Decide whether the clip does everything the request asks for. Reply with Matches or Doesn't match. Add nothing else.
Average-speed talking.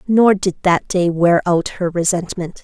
Matches